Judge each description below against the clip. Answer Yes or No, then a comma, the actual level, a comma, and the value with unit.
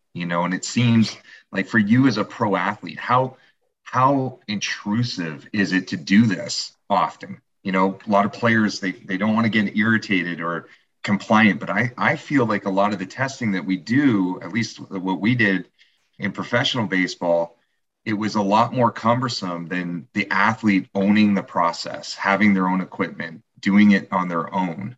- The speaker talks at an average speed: Yes, average, 185 wpm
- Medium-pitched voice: No, low, 100 Hz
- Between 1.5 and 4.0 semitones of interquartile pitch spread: Yes, average, 3.3 semitones